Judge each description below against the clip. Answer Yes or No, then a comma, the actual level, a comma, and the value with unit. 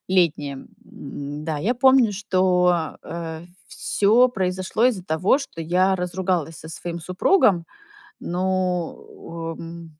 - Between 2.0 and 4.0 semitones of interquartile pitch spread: Yes, narrow, 2.4 semitones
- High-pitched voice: No, medium, 180 Hz